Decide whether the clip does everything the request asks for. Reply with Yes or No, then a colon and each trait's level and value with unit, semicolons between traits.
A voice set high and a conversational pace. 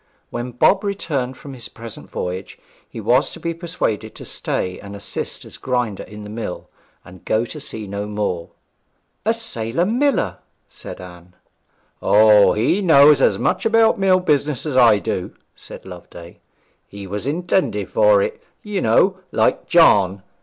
No: low, 125 Hz; average, 160 wpm